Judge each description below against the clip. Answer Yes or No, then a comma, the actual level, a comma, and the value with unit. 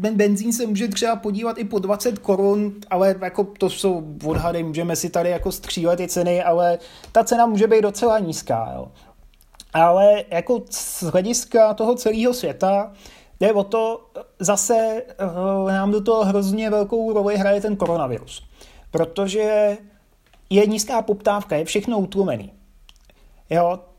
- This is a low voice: No, high, 200 Hz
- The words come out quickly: No, average, 145 wpm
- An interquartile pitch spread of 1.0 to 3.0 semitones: No, average, 3.5 semitones